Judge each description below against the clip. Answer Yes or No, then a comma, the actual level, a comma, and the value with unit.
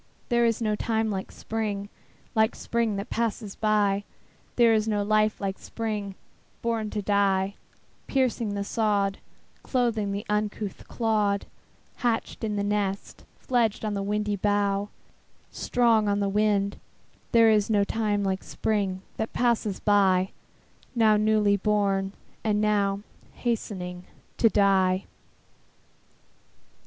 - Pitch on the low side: No, high, 210 Hz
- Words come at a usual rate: No, slow, 130 wpm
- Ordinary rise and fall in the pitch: No, narrow, 1.7 semitones